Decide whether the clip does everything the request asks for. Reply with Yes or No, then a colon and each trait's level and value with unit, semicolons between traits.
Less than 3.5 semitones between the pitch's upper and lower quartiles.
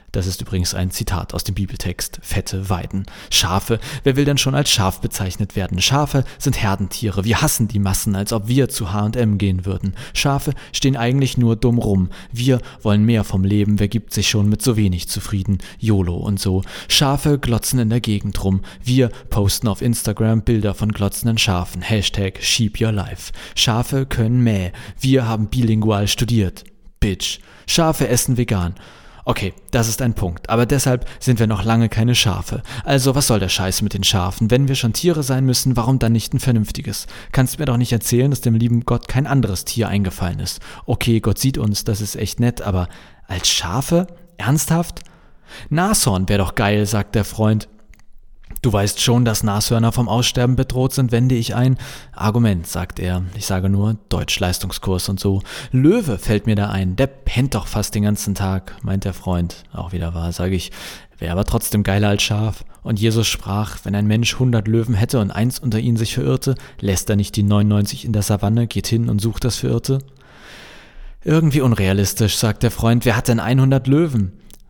No: average, 3.9 semitones